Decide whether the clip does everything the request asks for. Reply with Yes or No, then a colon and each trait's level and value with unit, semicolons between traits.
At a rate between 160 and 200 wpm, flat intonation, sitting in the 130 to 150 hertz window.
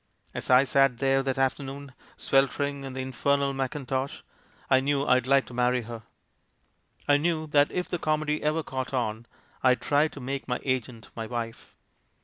Yes: average, 175 wpm; narrow, 2.1 semitones; low, 135 Hz